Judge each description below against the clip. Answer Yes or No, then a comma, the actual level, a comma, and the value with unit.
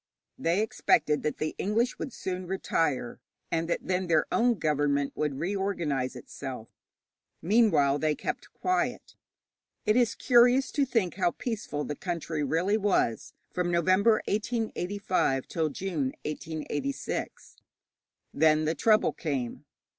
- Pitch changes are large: Yes, wide, 5.7 semitones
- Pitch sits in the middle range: Yes, medium, 170 Hz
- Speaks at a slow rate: Yes, slow, 125 wpm